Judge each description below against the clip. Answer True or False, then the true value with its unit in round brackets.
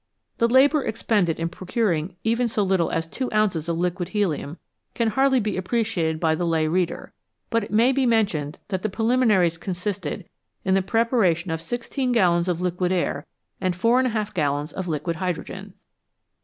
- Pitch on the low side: False (185 Hz)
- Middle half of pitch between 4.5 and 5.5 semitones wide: True (5.2 semitones)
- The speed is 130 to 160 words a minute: False (170 wpm)